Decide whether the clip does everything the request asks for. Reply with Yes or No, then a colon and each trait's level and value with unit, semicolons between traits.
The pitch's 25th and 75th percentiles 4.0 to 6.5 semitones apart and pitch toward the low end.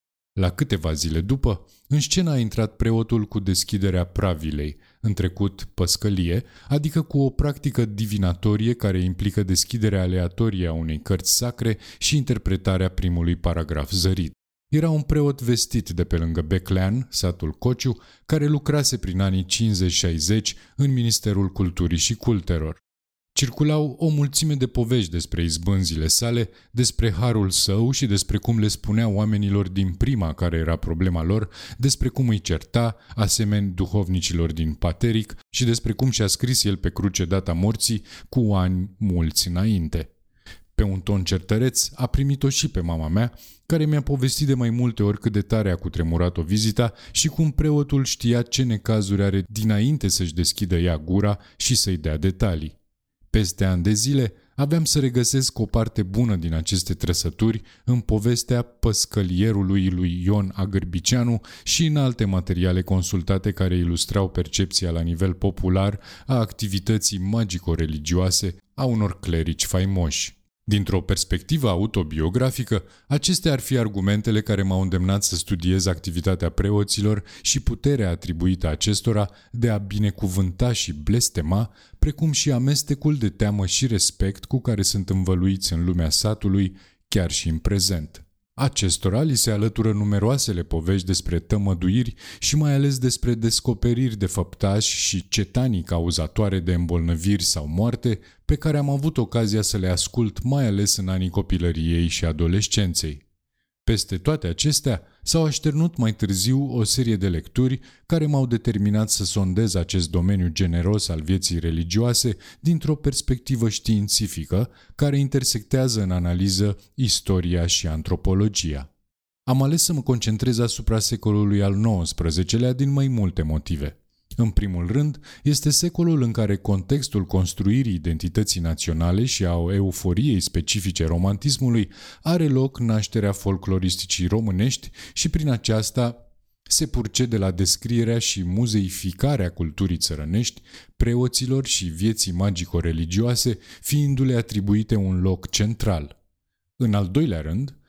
Yes: average, 4.7 semitones; low, 100 Hz